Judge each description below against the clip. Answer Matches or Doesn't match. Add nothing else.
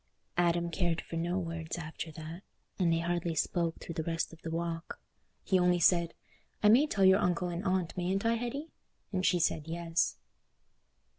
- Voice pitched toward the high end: Doesn't match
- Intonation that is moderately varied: Doesn't match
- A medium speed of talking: Matches